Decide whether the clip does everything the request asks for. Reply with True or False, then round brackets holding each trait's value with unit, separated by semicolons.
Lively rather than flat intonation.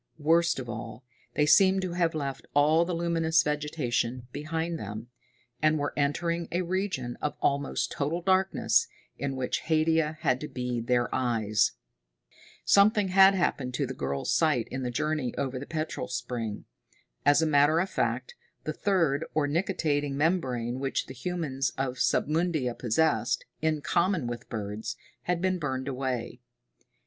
False (4.9 semitones)